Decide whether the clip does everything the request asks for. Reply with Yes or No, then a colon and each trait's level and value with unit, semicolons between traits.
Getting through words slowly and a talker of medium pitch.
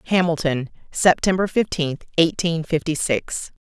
Yes: slow, 100 wpm; medium, 165 Hz